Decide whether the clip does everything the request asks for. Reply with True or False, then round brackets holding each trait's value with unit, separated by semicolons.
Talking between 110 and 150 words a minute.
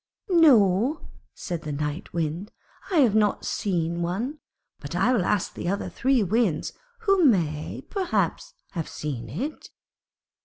True (140 wpm)